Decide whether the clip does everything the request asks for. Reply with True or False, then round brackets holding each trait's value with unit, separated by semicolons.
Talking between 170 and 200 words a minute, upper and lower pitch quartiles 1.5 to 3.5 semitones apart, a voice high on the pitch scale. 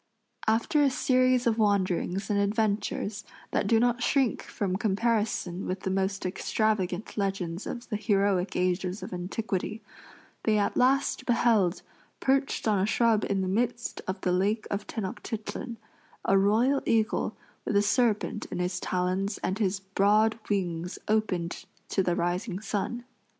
False (150 wpm; 3.0 semitones; 205 Hz)